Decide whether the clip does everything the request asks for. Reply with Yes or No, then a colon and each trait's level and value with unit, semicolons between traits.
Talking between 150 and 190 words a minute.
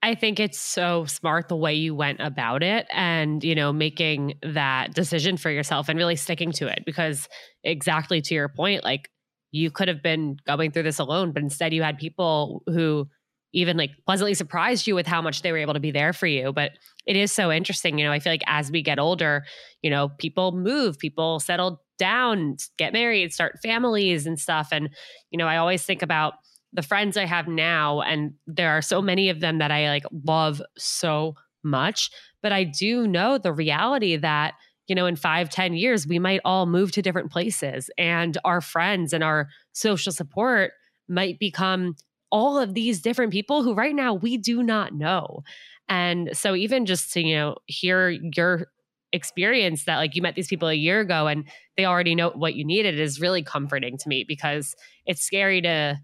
No: average, 200 wpm